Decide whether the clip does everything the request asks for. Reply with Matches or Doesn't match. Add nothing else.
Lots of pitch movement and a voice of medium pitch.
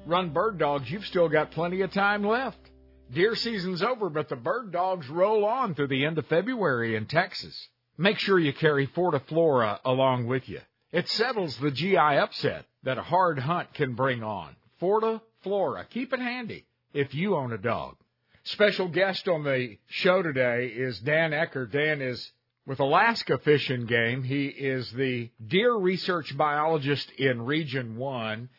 Matches